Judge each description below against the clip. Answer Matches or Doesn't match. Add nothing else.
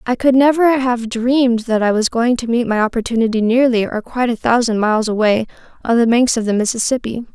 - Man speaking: Doesn't match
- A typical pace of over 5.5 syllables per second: Matches